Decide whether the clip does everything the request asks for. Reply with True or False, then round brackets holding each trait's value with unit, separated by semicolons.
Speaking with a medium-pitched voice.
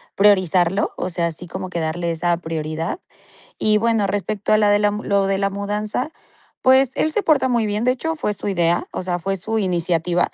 False (195 Hz)